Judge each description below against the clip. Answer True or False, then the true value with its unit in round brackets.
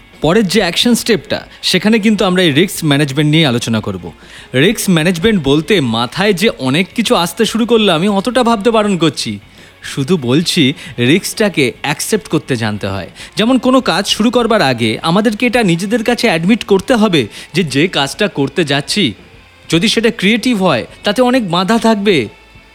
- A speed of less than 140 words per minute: False (160 wpm)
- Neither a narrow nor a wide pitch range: False (8.1 semitones)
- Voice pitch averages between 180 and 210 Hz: True (190 Hz)